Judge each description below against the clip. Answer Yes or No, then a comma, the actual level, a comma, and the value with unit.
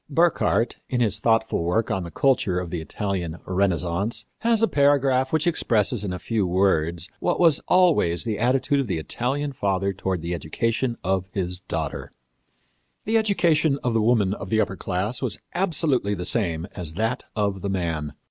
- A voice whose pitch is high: No, low, 105 Hz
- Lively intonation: Yes, wide, 6.3 semitones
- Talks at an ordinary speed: Yes, average, 175 wpm